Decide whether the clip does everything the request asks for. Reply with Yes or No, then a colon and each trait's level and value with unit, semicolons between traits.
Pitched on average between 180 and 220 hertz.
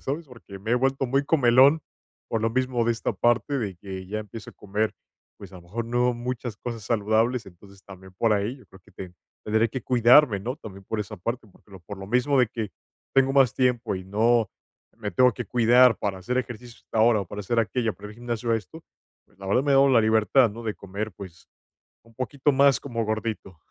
No: low, 115 Hz